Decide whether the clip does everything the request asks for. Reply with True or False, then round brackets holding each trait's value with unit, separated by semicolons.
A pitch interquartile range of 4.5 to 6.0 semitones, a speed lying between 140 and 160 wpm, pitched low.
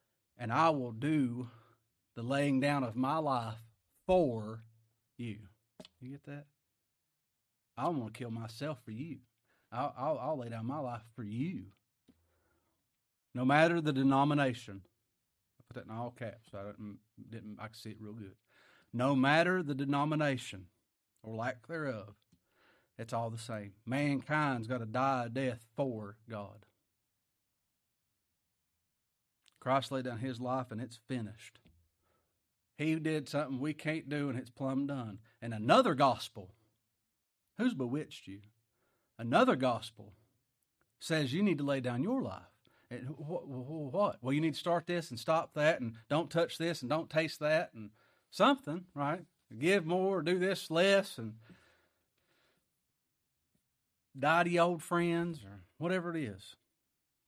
True (5.1 semitones; 150 wpm; 125 Hz)